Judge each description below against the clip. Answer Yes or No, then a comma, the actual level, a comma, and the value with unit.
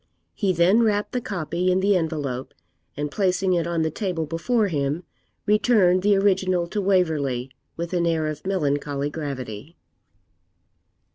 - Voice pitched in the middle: Yes, medium, 170 Hz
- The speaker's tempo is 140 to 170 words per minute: Yes, average, 145 wpm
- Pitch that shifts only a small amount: No, average, 4.4 semitones